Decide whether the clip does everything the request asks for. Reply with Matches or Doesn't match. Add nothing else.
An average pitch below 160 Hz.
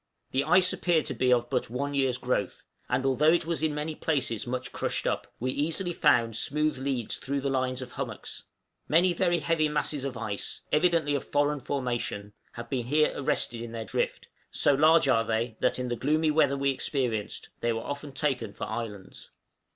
Matches